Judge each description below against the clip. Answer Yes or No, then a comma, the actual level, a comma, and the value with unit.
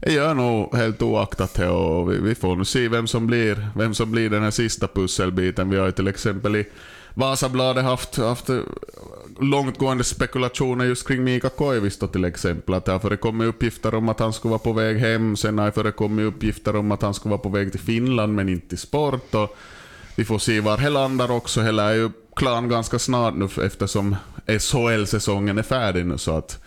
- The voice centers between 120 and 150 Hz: No, low, 110 Hz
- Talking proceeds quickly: Yes, fast, 200 wpm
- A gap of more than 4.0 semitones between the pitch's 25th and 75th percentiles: No, average, 3.4 semitones